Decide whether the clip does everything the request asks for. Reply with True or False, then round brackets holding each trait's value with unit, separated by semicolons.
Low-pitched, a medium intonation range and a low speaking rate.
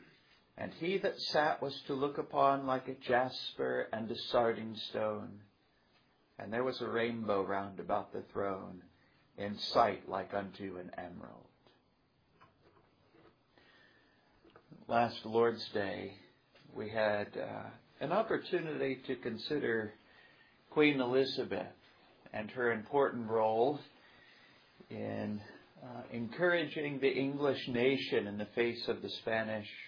True (120 Hz; 4.3 semitones; 115 wpm)